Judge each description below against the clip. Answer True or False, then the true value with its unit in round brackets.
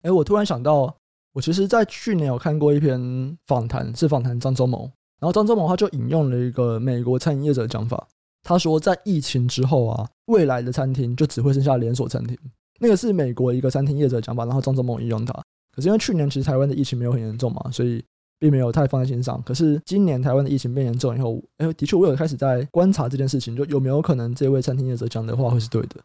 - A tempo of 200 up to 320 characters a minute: False (380 characters per minute)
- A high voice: False (135 Hz)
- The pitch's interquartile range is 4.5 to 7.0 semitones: False (3.8 semitones)